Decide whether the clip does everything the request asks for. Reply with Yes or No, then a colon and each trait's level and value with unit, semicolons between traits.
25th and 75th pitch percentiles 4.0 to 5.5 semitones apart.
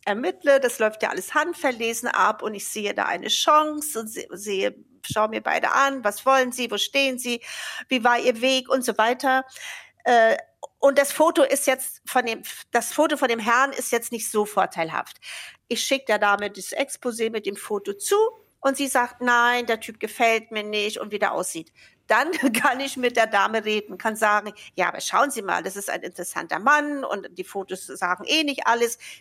Yes: average, 4.4 semitones